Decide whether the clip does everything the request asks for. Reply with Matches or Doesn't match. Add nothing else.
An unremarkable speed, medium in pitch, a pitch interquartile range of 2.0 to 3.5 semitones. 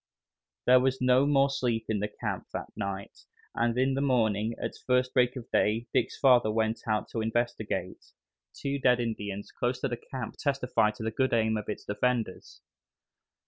Doesn't match